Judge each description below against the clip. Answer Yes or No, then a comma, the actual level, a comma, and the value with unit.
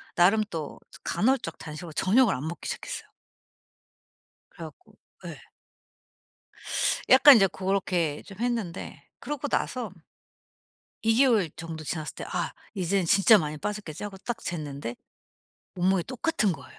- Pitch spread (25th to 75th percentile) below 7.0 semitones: Yes, wide, 5.6 semitones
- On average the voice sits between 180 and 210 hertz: Yes, high, 190 Hz